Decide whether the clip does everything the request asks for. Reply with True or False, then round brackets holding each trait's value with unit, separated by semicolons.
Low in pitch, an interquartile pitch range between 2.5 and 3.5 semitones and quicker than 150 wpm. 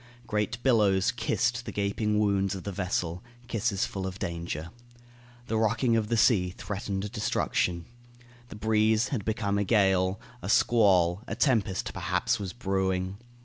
False (100 Hz; 2.9 semitones; 145 wpm)